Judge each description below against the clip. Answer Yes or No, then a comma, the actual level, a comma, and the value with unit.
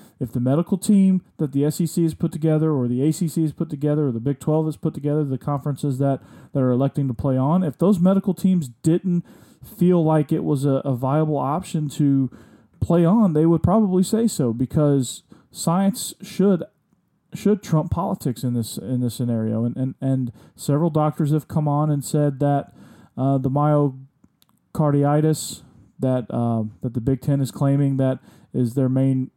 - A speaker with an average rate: Yes, average, 185 wpm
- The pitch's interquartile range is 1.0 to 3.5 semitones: No, average, 4.1 semitones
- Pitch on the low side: No, medium, 150 Hz